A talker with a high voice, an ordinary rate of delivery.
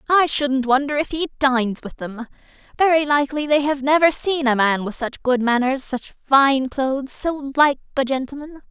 Yes: very high, 275 Hz; average, 185 wpm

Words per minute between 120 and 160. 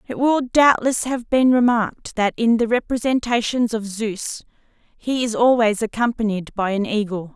Yes: average, 155 wpm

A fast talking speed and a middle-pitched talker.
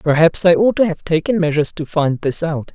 Yes: fast, 240 wpm; medium, 165 Hz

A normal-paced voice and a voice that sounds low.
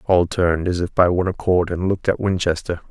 No: fast, 225 wpm; very low, 90 Hz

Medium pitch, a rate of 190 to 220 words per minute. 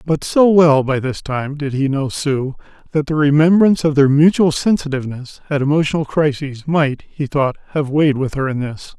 Yes: medium, 145 Hz; average, 195 wpm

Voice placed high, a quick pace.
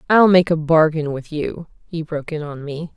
No: medium, 160 Hz; fast, 225 wpm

